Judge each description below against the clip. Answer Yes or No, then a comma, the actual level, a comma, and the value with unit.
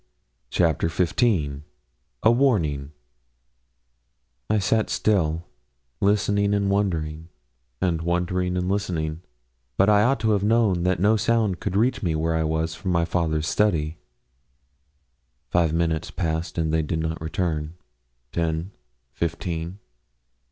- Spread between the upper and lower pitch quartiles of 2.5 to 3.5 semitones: No, average, 4.1 semitones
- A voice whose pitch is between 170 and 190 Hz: No, very low, 85 Hz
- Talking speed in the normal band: No, slow, 125 wpm